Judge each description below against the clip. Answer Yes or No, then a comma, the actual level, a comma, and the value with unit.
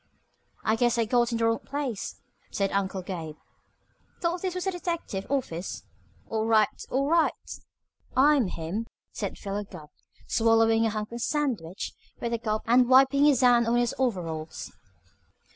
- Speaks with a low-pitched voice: No, high, 230 Hz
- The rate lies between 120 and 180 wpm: Yes, average, 160 wpm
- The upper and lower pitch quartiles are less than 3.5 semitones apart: No, average, 4.8 semitones